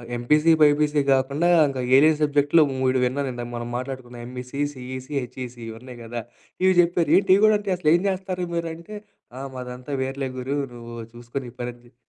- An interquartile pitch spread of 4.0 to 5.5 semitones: No, average, 3.5 semitones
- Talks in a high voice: No, low, 130 Hz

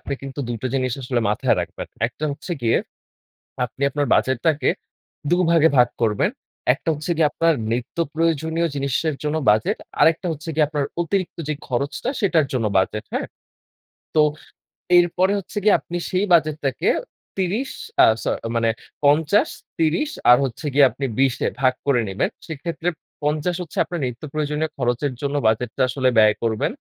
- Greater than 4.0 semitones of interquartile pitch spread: Yes, average, 4.7 semitones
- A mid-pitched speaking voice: Yes, medium, 150 Hz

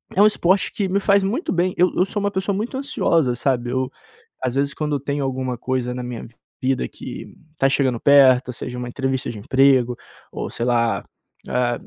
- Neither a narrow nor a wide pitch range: No, wide, 6.6 semitones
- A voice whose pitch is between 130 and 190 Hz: Yes, low, 135 Hz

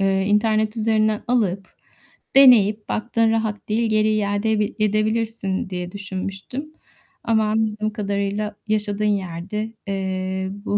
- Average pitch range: No, narrow, 1.9 semitones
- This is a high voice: Yes, high, 210 Hz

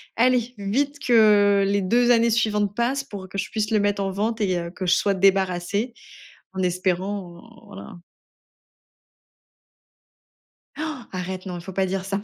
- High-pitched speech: Yes, high, 200 Hz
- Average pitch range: Yes, average, 3.4 semitones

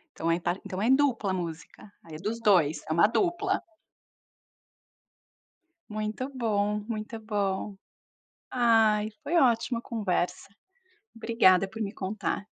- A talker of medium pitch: No, high, 215 Hz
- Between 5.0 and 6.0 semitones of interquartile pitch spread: No, average, 3.4 semitones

